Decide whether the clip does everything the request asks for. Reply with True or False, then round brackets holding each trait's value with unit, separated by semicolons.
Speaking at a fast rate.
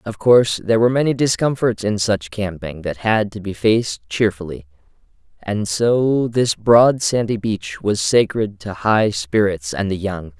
False (165 wpm)